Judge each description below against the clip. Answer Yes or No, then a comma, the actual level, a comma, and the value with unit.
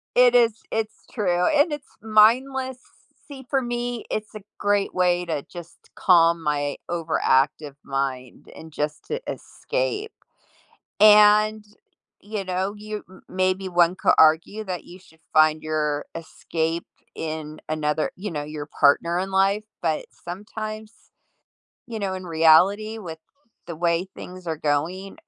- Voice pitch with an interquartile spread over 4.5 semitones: Yes, average, 5.1 semitones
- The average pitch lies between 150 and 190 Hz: Yes, medium, 185 Hz